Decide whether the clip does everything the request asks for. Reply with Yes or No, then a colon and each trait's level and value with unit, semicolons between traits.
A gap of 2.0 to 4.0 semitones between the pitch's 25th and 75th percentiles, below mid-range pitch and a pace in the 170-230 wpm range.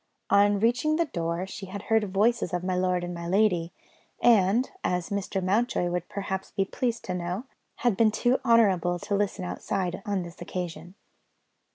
No: average, 3.4 semitones; high, 195 Hz; average, 180 wpm